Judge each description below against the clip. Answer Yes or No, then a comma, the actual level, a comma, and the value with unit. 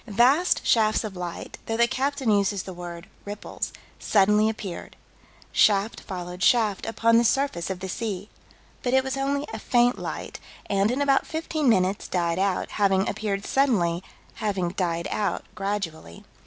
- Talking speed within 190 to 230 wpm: No, average, 155 wpm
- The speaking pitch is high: Yes, high, 205 Hz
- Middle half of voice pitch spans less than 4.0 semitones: No, average, 4.3 semitones